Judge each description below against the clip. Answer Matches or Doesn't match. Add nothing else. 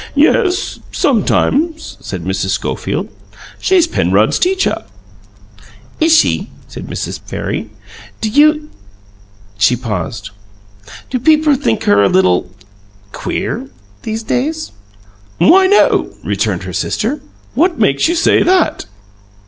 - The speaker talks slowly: Matches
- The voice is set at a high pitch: Matches